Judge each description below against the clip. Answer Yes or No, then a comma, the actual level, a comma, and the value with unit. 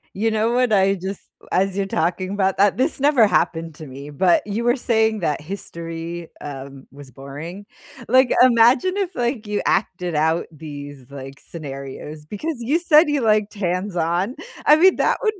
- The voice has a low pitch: No, high, 190 Hz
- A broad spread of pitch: Yes, wide, 6.9 semitones